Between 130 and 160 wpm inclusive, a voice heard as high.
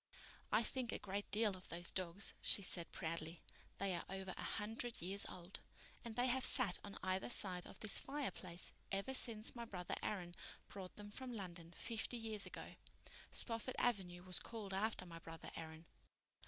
No: average, 175 wpm; high, 195 Hz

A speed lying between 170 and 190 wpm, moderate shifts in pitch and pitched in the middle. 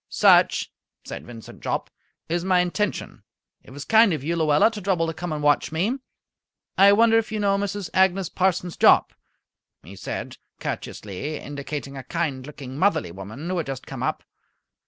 No: average, 175 wpm; wide, 5.7 semitones; medium, 165 Hz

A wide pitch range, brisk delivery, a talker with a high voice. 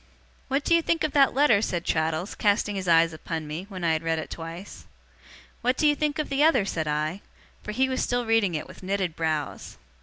Yes: wide, 8.3 semitones; fast, 225 wpm; high, 195 Hz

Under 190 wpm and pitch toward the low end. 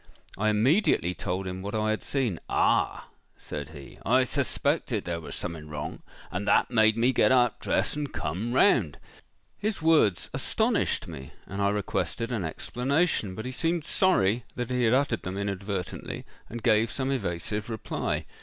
Yes: average, 160 wpm; low, 110 Hz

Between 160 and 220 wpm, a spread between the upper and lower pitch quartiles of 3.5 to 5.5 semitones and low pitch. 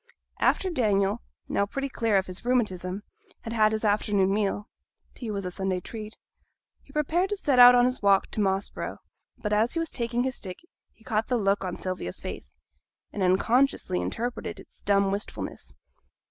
No: average, 180 wpm; average, 3.9 semitones; high, 210 Hz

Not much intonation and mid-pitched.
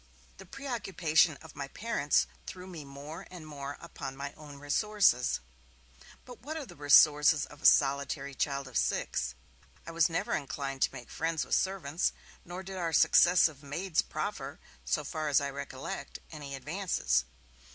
No: average, 4.1 semitones; medium, 150 Hz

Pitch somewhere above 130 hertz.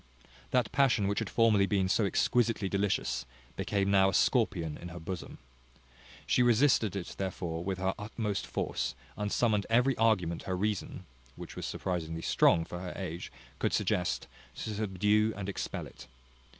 No: low, 100 Hz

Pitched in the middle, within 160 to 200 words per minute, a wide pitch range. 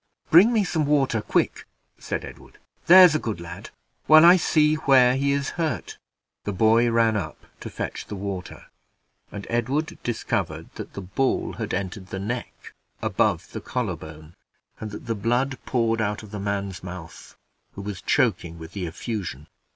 No: low, 110 Hz; average, 170 wpm; wide, 6.0 semitones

